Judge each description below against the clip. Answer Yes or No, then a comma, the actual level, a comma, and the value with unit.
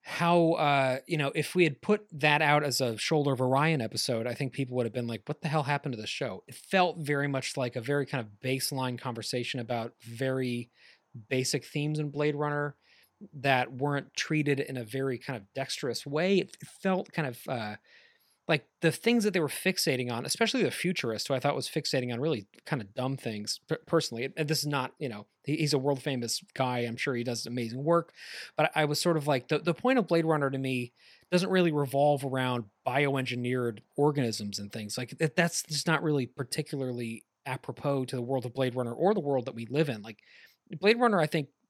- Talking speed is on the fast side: Yes, fast, 215 wpm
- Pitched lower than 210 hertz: Yes, medium, 140 Hz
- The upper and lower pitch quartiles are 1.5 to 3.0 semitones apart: No, average, 3.9 semitones